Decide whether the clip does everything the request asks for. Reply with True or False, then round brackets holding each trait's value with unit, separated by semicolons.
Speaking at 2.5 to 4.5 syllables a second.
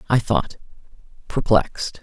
True (4.4 syllables/s)